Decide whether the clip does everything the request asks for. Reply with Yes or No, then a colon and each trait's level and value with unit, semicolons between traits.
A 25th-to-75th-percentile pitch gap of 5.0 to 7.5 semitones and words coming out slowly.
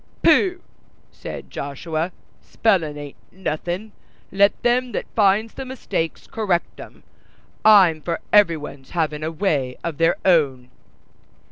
Yes: average, 5.3 semitones; slow, 125 wpm